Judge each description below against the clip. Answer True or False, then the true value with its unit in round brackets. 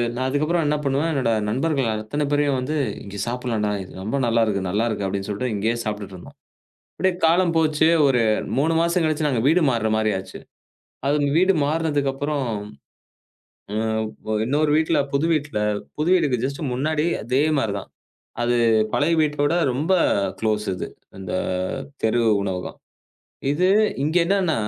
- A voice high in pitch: False (140 Hz)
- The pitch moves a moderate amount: False (5.8 semitones)